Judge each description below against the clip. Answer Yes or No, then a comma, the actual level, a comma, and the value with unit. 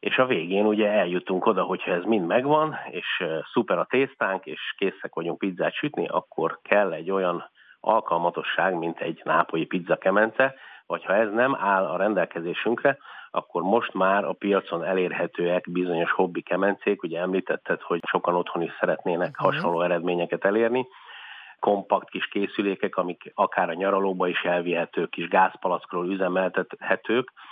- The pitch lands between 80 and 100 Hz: Yes, very low, 90 Hz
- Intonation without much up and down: No, average, 3.1 semitones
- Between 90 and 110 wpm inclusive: No, average, 145 wpm